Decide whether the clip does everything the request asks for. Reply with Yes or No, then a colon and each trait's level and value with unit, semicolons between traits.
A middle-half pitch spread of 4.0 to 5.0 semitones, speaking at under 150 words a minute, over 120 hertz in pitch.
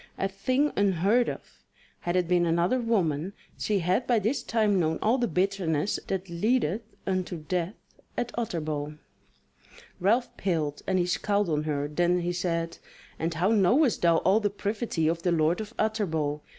No: average, 4.3 semitones; average, 165 wpm; medium, 185 Hz